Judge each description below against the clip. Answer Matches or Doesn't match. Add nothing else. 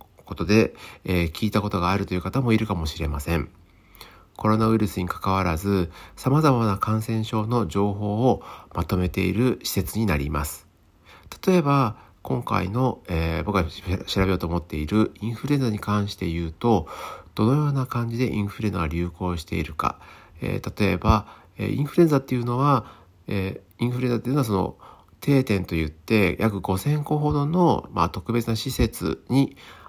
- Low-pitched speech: Matches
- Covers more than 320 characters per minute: Matches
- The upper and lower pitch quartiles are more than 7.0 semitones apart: Doesn't match